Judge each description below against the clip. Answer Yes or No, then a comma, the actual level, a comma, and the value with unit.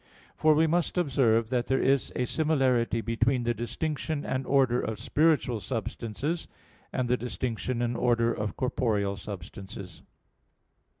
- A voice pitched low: Yes, low, 120 Hz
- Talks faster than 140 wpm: No, slow, 135 wpm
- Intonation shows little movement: No, average, 3.2 semitones